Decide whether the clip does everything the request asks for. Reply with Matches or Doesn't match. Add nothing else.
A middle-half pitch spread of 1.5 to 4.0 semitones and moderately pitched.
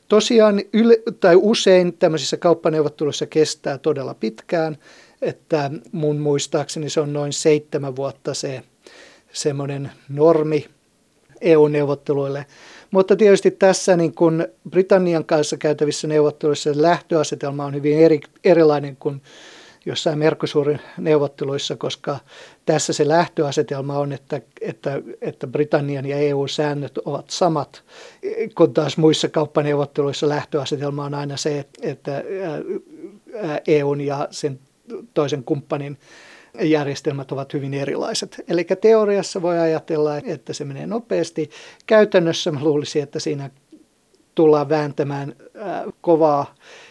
Matches